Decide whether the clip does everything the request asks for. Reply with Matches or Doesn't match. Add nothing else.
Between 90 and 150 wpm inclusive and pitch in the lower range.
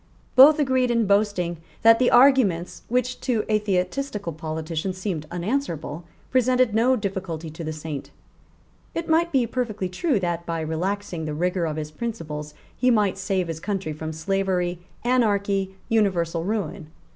Doesn't match